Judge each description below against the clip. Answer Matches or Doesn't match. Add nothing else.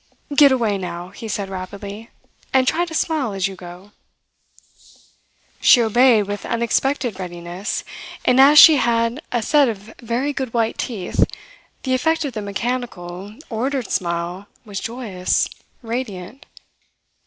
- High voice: Matches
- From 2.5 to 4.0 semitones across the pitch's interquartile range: Doesn't match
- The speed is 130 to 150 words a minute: Matches